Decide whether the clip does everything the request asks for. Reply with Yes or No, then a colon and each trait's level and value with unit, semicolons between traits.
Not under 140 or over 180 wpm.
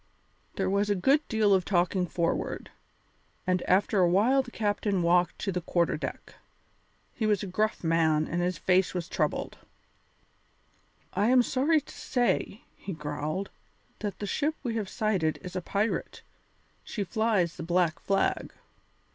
Yes: average, 155 wpm